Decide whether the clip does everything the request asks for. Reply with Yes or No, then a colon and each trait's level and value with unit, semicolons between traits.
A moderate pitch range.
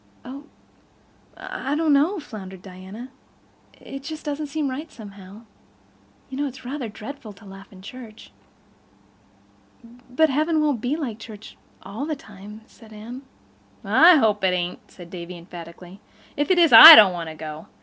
No: wide, 6.8 semitones